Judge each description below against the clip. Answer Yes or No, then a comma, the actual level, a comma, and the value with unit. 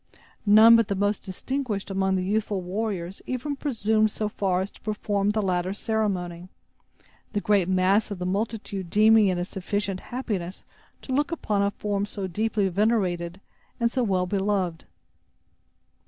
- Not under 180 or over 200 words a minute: No, average, 155 wpm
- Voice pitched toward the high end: Yes, high, 200 Hz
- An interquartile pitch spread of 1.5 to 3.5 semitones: Yes, narrow, 2.6 semitones